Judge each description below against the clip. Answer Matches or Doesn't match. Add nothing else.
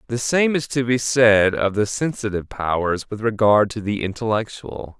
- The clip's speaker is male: Matches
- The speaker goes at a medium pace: Matches